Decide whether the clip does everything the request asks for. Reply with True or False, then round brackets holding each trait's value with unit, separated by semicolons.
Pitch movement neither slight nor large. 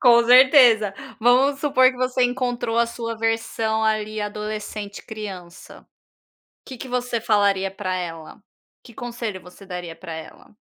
True (3.3 semitones)